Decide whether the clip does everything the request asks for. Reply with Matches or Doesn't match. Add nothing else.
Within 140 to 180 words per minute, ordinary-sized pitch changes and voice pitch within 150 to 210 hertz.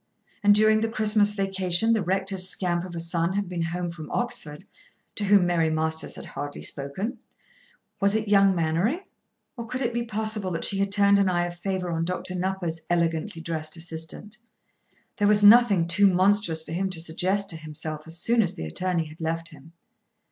Doesn't match